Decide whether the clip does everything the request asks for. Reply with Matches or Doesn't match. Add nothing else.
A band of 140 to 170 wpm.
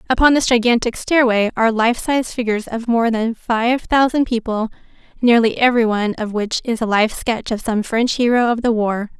Doesn't match